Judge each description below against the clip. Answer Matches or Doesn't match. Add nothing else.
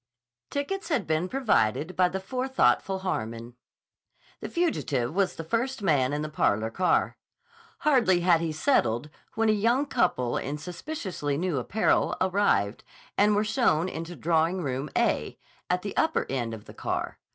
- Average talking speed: Matches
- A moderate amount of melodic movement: Doesn't match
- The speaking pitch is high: Doesn't match